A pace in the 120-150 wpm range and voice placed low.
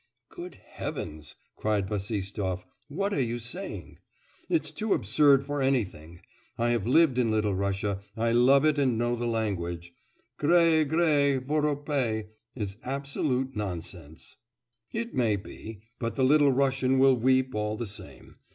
Yes: average, 140 wpm; low, 120 Hz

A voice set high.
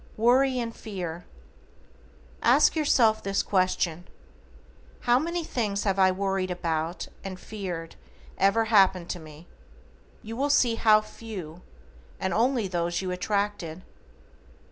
Yes: high, 195 Hz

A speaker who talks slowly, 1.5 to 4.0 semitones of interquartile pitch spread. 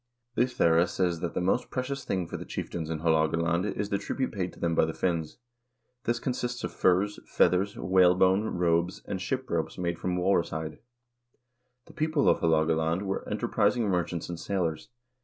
No: average, 175 wpm; average, 3.5 semitones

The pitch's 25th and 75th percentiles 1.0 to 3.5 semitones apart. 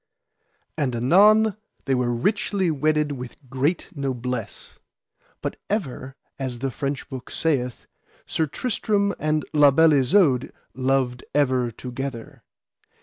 No: average, 4.1 semitones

